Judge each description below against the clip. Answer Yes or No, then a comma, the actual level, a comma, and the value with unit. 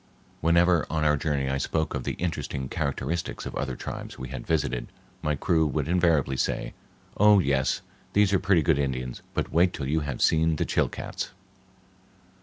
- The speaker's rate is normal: Yes, average, 175 wpm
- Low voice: Yes, very low, 75 Hz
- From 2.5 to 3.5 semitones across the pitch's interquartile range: No, average, 4.0 semitones